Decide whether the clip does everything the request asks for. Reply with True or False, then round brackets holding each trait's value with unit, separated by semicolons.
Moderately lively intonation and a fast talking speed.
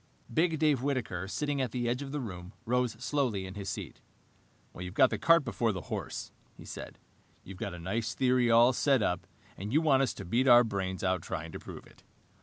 False (5.9 semitones; 215 wpm)